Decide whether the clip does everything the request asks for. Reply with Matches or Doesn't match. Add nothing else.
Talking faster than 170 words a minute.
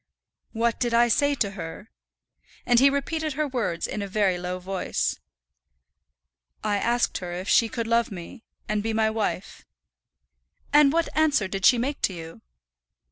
Doesn't match